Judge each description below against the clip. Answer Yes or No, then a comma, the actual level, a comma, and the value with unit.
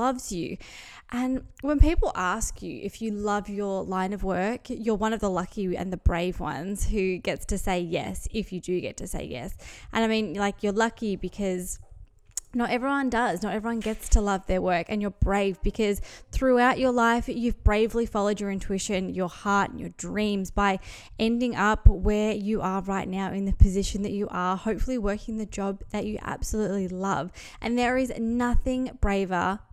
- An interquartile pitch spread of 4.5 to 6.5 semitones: No, average, 3.0 semitones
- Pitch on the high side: Yes, high, 205 Hz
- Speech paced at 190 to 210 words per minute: Yes, average, 195 wpm